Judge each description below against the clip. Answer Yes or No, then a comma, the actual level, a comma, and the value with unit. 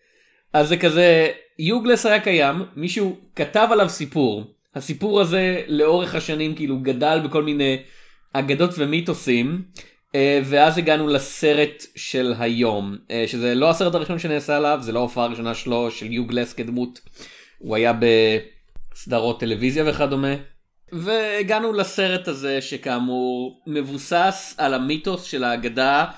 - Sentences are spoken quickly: No, average, 120 wpm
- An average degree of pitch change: No, wide, 6.0 semitones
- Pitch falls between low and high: Yes, medium, 145 Hz